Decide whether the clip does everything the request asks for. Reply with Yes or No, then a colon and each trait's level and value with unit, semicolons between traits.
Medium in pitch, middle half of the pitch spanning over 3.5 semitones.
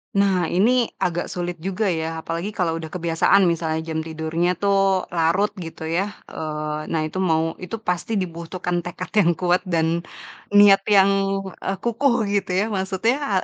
No: medium, 180 Hz; average, 3.2 semitones